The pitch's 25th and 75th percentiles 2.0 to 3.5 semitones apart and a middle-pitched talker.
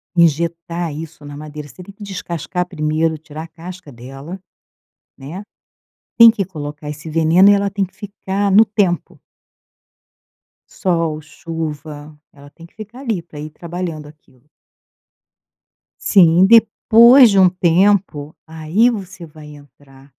No: average, 4.3 semitones; medium, 165 Hz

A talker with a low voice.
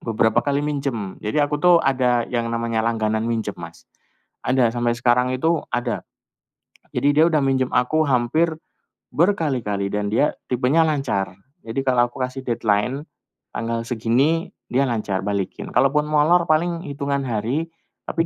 Yes: low, 125 Hz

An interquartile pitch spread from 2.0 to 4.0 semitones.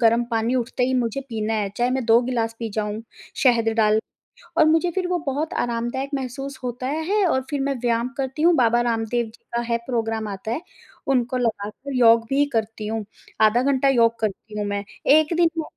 Yes: average, 3.3 semitones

